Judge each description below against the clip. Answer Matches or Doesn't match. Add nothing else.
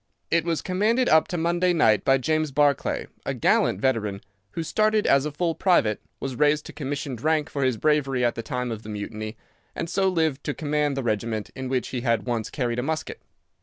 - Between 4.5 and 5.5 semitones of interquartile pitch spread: Matches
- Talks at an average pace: Doesn't match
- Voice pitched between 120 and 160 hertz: Matches